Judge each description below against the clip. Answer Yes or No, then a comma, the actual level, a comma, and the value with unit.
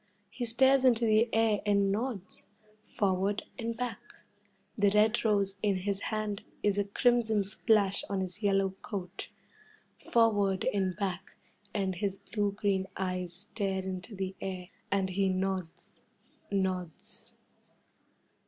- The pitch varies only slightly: Yes, narrow, 2.2 semitones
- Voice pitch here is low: No, high, 200 Hz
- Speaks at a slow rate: Yes, slow, 130 wpm